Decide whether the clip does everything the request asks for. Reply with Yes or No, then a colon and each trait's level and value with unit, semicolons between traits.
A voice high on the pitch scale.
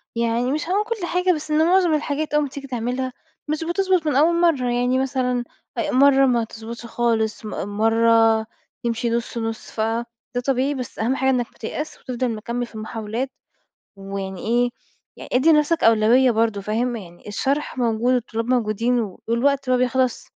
Yes: high, 245 Hz